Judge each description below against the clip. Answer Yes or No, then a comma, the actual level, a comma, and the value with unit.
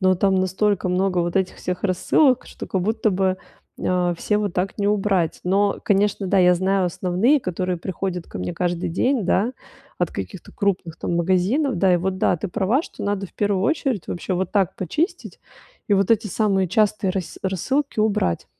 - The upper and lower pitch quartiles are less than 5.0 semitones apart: Yes, narrow, 2.4 semitones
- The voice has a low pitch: No, high, 190 Hz